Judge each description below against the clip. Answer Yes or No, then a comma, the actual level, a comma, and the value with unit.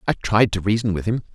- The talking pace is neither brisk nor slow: No, fast, 270 wpm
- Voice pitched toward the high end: No, low, 105 Hz